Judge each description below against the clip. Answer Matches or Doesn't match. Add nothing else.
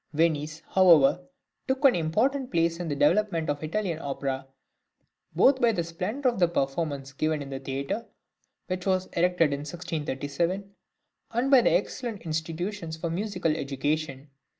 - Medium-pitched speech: Matches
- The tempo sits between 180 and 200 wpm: Doesn't match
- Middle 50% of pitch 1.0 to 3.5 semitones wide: Doesn't match